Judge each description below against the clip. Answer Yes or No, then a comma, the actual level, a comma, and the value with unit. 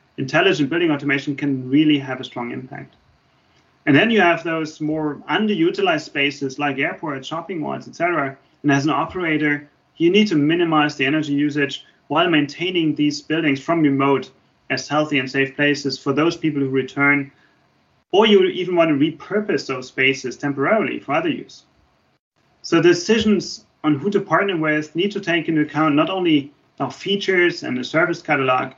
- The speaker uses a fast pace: No, average, 170 wpm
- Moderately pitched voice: Yes, medium, 150 Hz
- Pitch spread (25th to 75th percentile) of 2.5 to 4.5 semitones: Yes, average, 3.5 semitones